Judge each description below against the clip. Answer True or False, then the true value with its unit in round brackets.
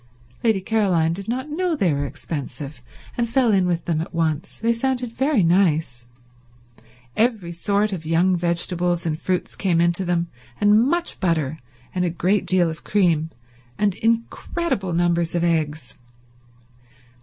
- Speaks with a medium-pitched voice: True (180 Hz)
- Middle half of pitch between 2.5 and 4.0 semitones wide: False (4.5 semitones)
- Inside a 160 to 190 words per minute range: False (150 wpm)